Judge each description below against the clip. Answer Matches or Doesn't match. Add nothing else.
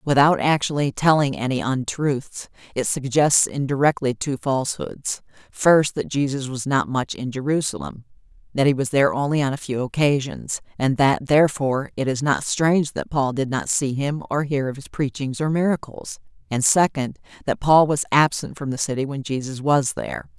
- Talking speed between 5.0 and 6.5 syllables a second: Matches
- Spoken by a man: Doesn't match